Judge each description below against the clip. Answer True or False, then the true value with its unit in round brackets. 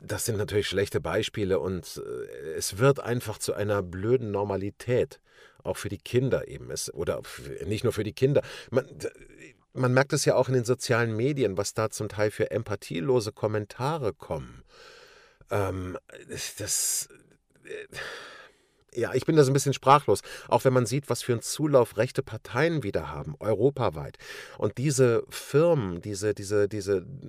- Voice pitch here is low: True (125 Hz)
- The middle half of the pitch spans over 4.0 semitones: True (5.2 semitones)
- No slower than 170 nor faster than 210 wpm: False (160 wpm)